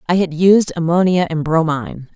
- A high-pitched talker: No, medium, 170 Hz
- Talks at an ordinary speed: Yes, average, 165 wpm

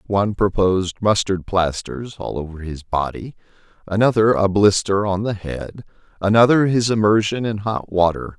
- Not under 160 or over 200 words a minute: No, average, 145 wpm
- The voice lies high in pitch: No, low, 100 Hz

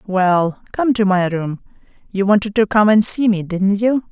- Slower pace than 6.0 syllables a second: Yes, 4.5 syllables/s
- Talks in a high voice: Yes, high, 200 Hz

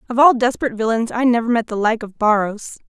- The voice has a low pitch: No, high, 230 Hz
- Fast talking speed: Yes, fast, 225 wpm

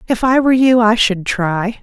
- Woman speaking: Yes, female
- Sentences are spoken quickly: Yes, fast, 230 wpm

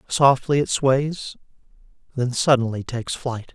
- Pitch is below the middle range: Yes, low, 130 Hz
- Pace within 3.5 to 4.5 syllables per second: Yes, 4.2 syllables/s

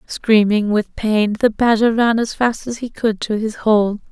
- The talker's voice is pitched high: Yes, high, 220 Hz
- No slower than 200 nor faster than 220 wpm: Yes, fast, 205 wpm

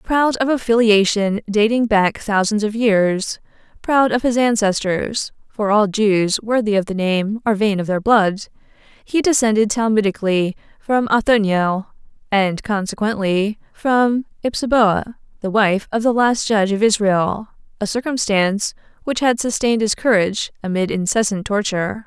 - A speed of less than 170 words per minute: Yes, slow, 135 wpm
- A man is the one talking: No, female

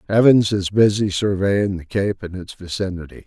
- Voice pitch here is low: Yes, very low, 95 Hz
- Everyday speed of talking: Yes, average, 165 wpm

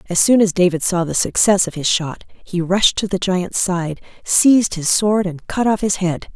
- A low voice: No, medium, 185 Hz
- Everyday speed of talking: No, fast, 225 wpm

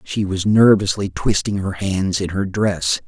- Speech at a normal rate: Yes, average, 175 wpm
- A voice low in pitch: Yes, low, 100 Hz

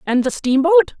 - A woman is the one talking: Yes, female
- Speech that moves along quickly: No, average, 180 wpm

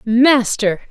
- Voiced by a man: No, female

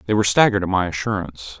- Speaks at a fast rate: Yes, fast, 225 wpm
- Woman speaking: No, male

